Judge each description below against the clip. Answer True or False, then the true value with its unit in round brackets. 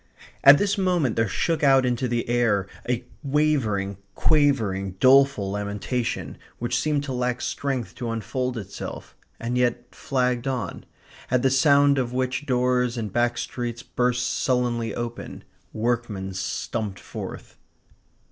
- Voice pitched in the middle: False (125 Hz)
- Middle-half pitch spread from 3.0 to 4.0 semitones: False (2.5 semitones)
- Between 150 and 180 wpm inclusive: False (135 wpm)